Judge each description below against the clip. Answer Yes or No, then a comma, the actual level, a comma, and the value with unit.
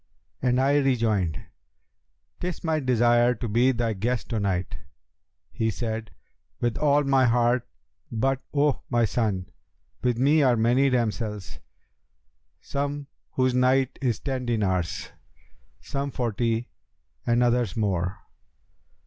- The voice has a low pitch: Yes, low, 120 Hz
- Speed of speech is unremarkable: No, slow, 120 wpm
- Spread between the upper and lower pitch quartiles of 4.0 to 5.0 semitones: No, average, 3.1 semitones